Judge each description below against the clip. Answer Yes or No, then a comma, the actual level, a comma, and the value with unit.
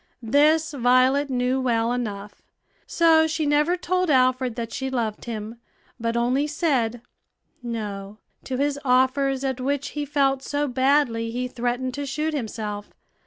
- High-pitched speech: Yes, very high, 260 Hz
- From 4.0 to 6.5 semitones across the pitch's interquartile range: No, average, 3.4 semitones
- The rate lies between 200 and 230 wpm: No, average, 145 wpm